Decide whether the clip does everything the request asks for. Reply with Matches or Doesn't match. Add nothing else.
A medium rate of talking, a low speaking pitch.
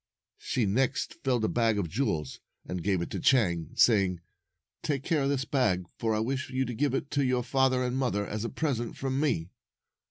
Doesn't match